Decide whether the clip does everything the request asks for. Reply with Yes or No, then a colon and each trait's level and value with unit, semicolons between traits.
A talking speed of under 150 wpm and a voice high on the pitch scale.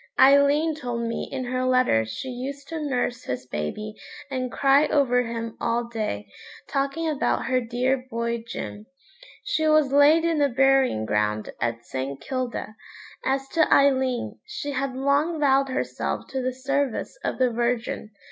No: average, 155 wpm; very high, 255 Hz